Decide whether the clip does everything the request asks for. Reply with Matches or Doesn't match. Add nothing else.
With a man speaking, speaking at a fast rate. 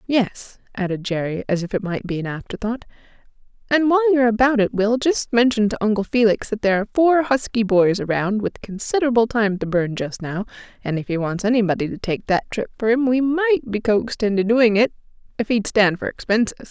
Doesn't match